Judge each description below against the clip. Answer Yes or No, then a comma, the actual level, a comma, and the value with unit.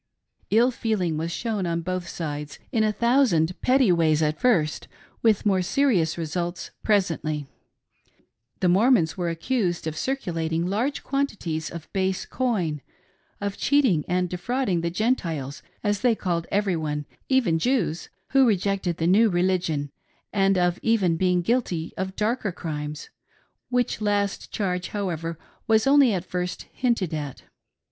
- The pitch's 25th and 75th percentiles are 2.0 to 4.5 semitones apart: No, average, 5.1 semitones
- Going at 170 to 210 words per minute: No, average, 150 wpm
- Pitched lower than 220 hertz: Yes, medium, 185 Hz